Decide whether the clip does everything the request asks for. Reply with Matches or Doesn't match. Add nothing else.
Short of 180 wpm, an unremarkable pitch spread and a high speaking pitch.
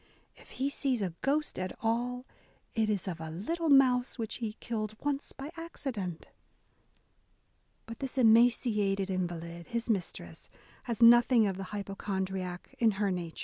Matches